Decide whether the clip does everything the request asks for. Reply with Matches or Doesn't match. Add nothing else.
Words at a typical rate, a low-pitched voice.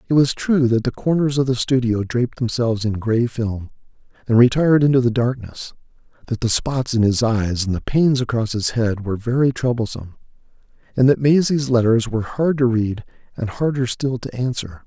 Matches